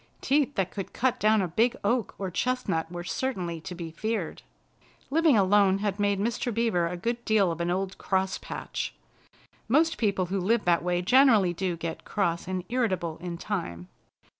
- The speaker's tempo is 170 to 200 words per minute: Yes, average, 180 wpm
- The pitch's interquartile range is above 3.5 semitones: Yes, average, 4.5 semitones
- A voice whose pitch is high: Yes, high, 195 Hz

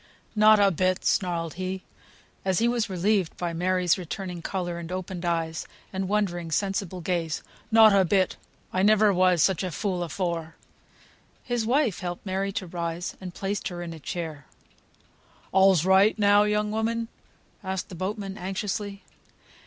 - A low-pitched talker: No, medium, 185 Hz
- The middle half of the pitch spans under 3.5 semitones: Yes, narrow, 2.6 semitones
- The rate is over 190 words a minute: No, average, 155 wpm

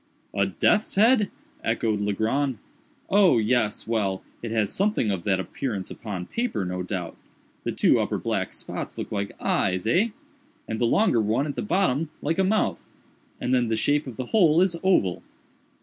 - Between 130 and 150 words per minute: No, average, 165 wpm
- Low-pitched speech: Yes, low, 115 Hz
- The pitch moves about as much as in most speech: No, wide, 9.0 semitones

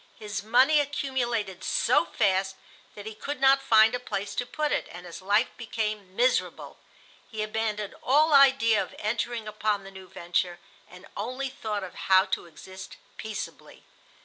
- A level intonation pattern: No, average, 4.4 semitones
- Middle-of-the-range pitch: No, high, 215 Hz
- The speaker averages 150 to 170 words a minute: Yes, average, 160 wpm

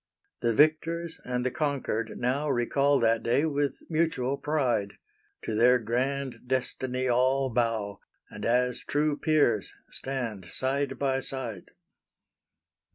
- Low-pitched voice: Yes, low, 130 Hz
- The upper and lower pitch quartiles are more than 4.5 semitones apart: No, average, 3.2 semitones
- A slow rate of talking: Yes, slow, 120 wpm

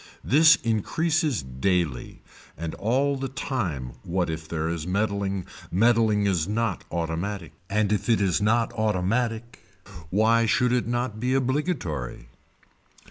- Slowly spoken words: Yes, slow, 125 wpm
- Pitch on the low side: Yes, low, 105 Hz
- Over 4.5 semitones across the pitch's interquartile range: Yes, wide, 5.5 semitones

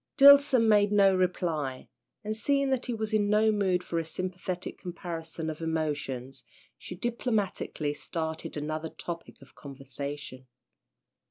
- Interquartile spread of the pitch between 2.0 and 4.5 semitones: No, wide, 5.5 semitones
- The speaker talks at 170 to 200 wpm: No, slow, 135 wpm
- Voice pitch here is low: No, medium, 175 Hz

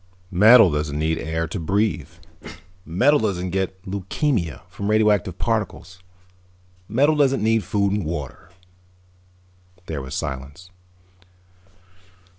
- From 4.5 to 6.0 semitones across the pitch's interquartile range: Yes, average, 4.9 semitones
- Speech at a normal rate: No, slow, 105 wpm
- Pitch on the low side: Yes, very low, 95 Hz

